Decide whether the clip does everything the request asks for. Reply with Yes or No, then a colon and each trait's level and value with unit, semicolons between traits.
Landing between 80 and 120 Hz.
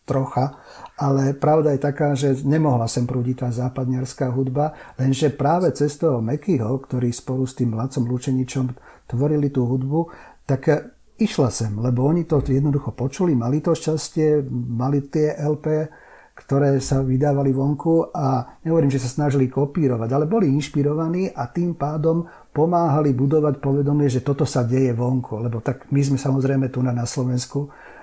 No: medium, 140 Hz